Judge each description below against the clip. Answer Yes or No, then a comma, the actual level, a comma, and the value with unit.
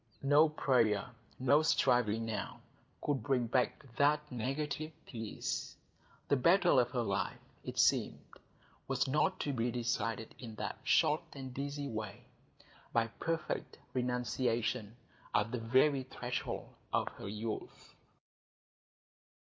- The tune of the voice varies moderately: Yes, average, 3.9 semitones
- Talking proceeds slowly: Yes, slow, 115 wpm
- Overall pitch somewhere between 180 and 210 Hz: No, low, 125 Hz